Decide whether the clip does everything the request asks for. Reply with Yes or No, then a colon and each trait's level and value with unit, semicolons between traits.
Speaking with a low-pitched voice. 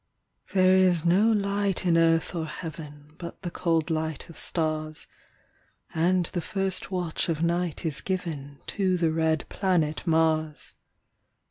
No: medium, 165 Hz